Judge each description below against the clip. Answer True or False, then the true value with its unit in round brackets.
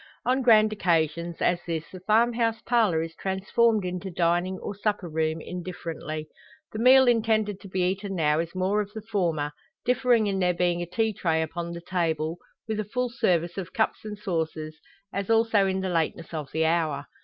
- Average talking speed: True (190 wpm)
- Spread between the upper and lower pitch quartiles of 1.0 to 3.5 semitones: False (4.5 semitones)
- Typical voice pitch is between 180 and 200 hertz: True (185 Hz)